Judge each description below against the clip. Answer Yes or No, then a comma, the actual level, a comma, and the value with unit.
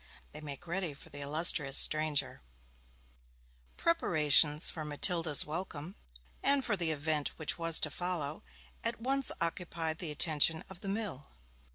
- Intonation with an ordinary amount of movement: Yes, average, 3.1 semitones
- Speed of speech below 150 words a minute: Yes, average, 140 wpm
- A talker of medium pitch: Yes, medium, 160 Hz